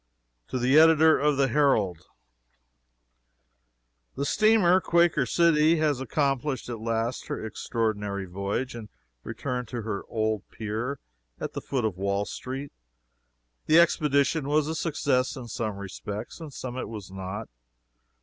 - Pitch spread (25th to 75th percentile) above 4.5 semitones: Yes, wide, 5.5 semitones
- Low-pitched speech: Yes, low, 125 Hz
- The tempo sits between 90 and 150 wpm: Yes, average, 140 wpm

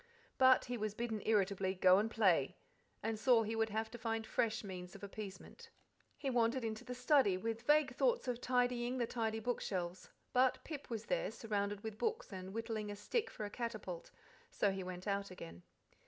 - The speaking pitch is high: Yes, high, 220 Hz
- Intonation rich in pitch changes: No, average, 3.6 semitones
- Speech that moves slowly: No, average, 190 wpm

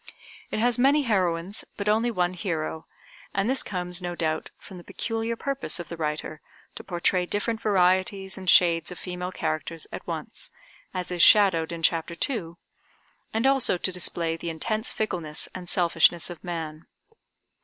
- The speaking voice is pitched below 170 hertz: No, medium, 180 Hz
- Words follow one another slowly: No, average, 165 wpm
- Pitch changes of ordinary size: Yes, average, 3.9 semitones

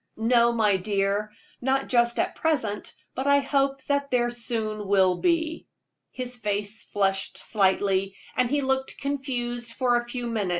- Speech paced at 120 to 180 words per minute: Yes, average, 155 wpm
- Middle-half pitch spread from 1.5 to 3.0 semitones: No, average, 4.4 semitones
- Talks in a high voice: Yes, high, 240 Hz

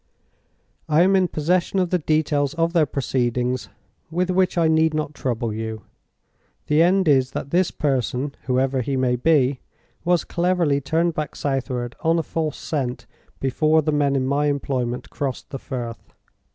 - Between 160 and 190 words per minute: Yes, average, 165 wpm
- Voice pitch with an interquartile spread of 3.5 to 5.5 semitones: Yes, average, 4.1 semitones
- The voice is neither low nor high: Yes, medium, 145 Hz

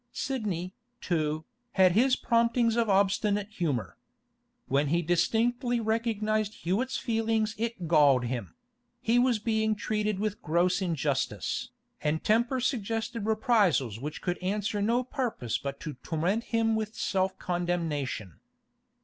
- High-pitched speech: Yes, high, 205 Hz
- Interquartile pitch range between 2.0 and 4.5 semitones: No, average, 5.3 semitones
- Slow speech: Yes, slow, 125 wpm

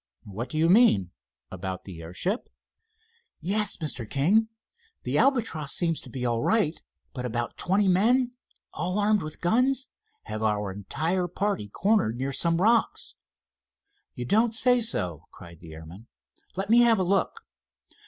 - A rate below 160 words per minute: Yes, average, 145 wpm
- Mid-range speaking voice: Yes, medium, 170 Hz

